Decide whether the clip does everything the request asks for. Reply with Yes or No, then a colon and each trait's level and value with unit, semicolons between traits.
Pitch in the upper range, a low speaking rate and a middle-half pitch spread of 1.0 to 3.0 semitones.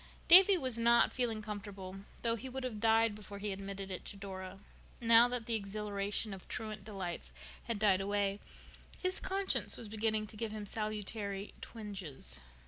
No: high, 210 Hz; average, 165 wpm; narrow, 2.5 semitones